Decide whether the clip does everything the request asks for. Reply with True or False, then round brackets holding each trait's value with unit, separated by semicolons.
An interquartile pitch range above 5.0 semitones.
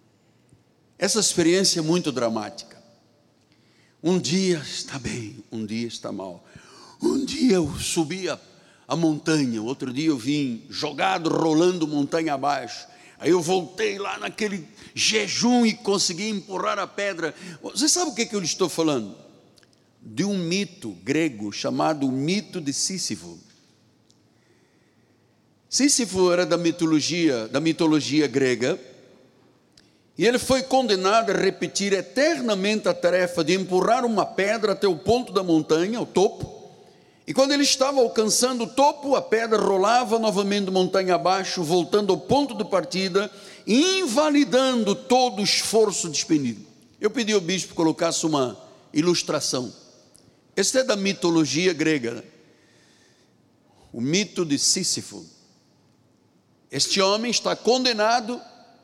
True (5.4 semitones)